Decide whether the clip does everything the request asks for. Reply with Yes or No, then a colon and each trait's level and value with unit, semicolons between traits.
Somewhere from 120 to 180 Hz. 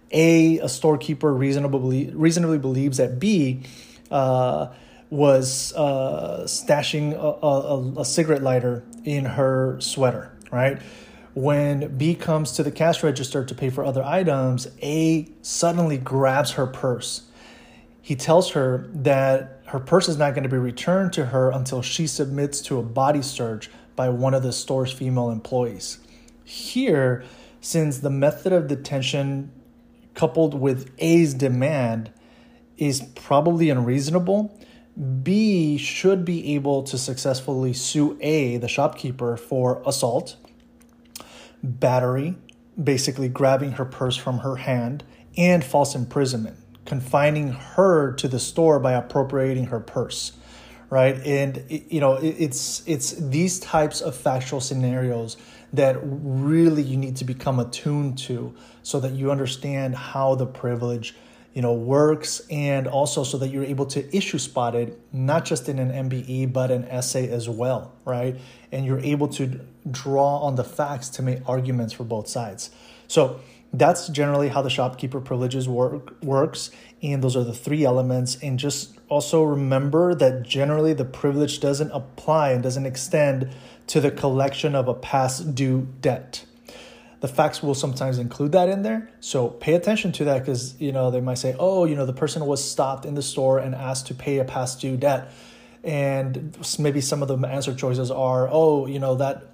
Yes: low, 135 Hz